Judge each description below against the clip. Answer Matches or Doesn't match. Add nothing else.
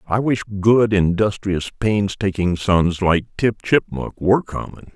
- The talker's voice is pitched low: Matches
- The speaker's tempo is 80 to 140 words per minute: Matches